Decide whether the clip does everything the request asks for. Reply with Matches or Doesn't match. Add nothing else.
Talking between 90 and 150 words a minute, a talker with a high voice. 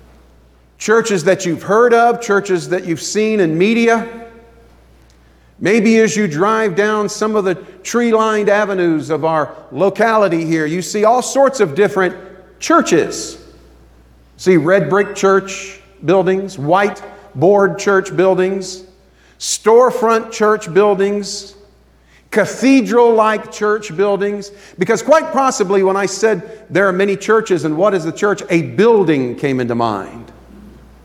Matches